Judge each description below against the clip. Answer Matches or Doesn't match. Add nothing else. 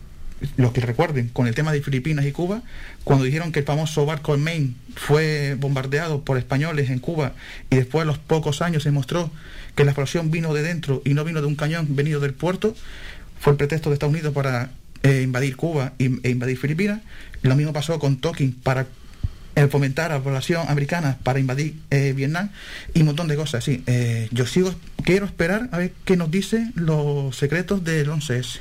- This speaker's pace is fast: Matches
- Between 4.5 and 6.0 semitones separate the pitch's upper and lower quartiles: Doesn't match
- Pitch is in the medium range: Matches